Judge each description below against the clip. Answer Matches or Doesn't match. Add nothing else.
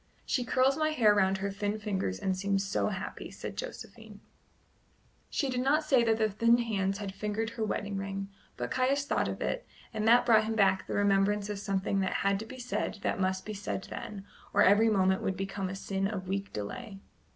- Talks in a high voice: Matches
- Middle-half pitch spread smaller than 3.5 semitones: Matches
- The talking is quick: Matches